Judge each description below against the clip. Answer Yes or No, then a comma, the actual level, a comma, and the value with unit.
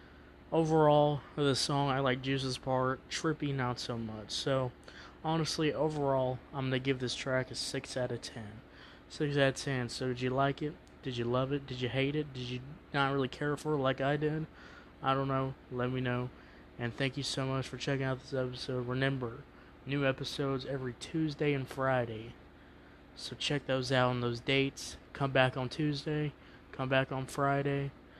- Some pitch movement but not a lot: No, narrow, 1.9 semitones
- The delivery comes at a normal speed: Yes, average, 190 wpm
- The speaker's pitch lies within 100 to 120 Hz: No, low, 135 Hz